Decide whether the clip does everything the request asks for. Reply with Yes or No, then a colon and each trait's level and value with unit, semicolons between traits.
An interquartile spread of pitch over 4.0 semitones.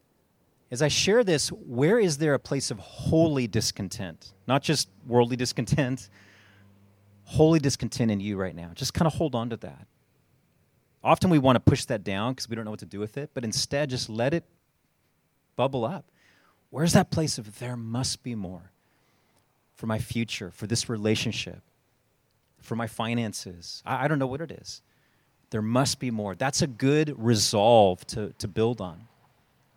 Yes: average, 4.4 semitones